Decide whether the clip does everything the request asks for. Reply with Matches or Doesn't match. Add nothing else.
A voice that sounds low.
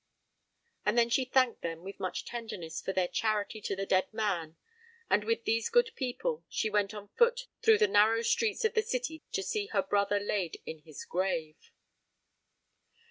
Doesn't match